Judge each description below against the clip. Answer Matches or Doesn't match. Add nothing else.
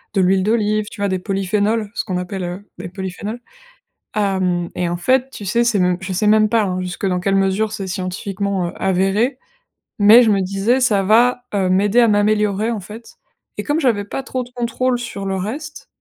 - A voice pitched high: Matches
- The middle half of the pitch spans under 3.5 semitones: Matches